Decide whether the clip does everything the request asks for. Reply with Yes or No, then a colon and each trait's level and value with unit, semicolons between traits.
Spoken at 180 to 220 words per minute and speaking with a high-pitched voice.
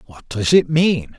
No: average, 200 wpm; low, 135 Hz